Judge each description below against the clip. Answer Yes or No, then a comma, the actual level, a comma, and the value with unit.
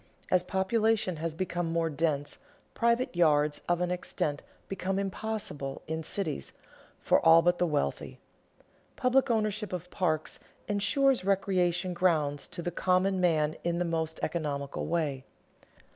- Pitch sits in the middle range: Yes, medium, 175 Hz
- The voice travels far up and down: No, average, 3.5 semitones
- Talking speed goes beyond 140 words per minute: No, slow, 135 wpm